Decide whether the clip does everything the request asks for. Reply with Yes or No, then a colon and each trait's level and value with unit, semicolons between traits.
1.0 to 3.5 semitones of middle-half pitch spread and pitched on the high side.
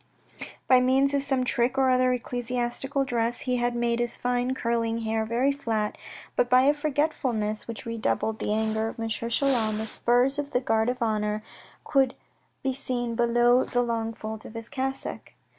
Yes: narrow, 2.4 semitones; high, 240 Hz